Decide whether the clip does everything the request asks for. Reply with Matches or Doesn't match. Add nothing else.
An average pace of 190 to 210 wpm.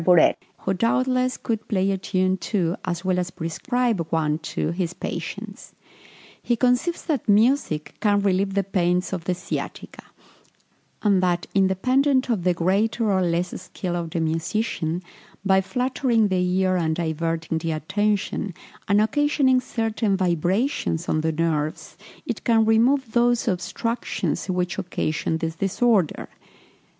Doesn't match